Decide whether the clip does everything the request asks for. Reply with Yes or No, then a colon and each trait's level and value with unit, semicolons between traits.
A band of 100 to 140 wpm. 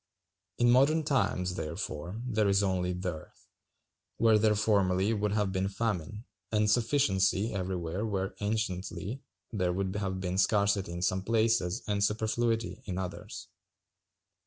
Yes: slow, 135 wpm